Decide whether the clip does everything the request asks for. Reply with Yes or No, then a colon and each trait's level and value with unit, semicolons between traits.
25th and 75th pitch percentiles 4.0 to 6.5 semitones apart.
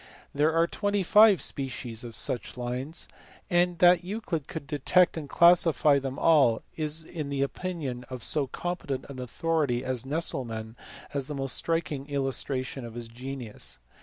Yes: average, 4.4 semitones